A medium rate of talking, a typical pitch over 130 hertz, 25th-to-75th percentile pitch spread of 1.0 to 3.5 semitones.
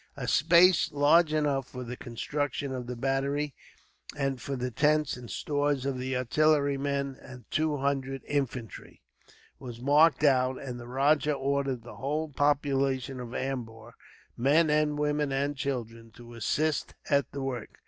Yes: average, 150 wpm; medium, 140 Hz; narrow, 2.5 semitones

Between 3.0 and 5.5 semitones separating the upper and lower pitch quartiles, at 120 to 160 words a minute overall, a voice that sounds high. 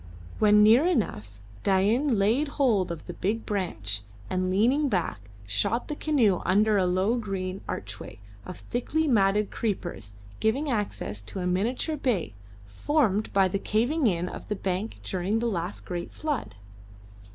Yes: average, 4.7 semitones; average, 150 wpm; high, 200 Hz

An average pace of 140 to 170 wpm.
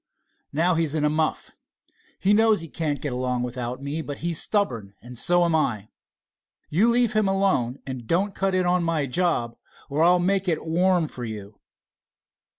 No: average, 180 wpm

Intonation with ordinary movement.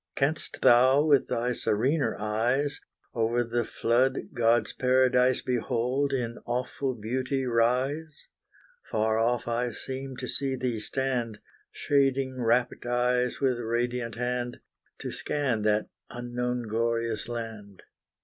No: narrow, 2.0 semitones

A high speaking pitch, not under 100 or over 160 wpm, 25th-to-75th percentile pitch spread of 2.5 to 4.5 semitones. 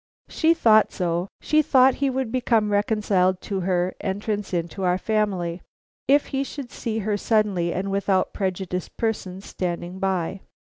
Yes: high, 200 Hz; average, 150 wpm; average, 3.4 semitones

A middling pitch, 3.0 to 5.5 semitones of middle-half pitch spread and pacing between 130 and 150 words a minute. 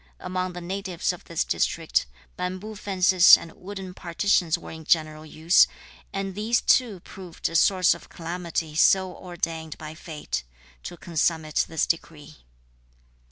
No: medium, 175 Hz; narrow, 2.6 semitones; average, 140 wpm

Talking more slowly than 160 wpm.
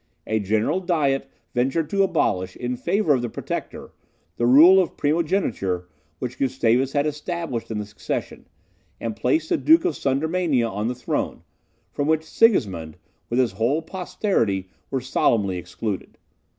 Yes: average, 150 wpm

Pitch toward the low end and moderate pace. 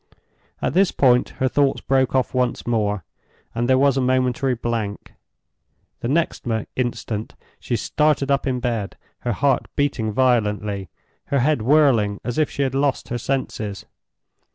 Yes: low, 125 Hz; average, 155 wpm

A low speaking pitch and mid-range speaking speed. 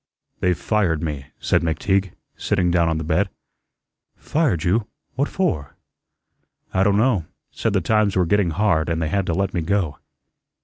Yes: very low, 90 Hz; average, 170 wpm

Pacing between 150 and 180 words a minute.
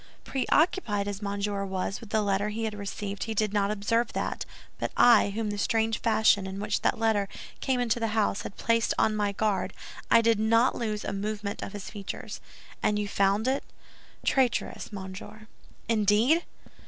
Yes: average, 175 wpm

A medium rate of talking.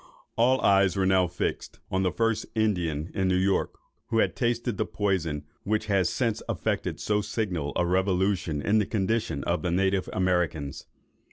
Yes: average, 170 wpm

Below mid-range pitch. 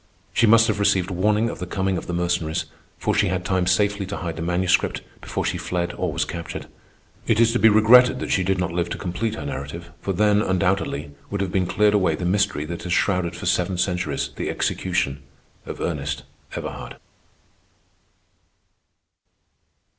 Yes: very low, 90 Hz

